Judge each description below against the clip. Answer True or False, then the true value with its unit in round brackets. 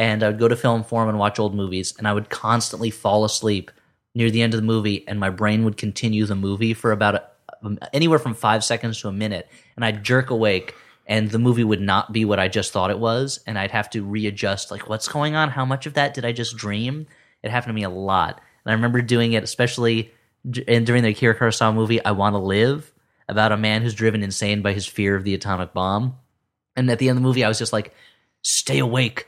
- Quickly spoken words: True (245 wpm)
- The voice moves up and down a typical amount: False (2.3 semitones)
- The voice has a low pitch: True (110 Hz)